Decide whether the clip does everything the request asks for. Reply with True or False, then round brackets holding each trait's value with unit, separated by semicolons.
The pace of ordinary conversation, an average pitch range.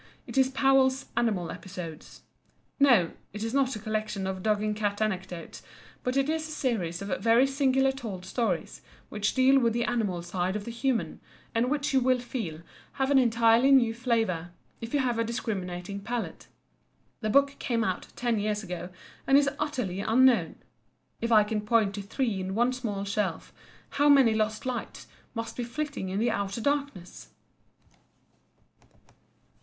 True (170 wpm; 4.6 semitones)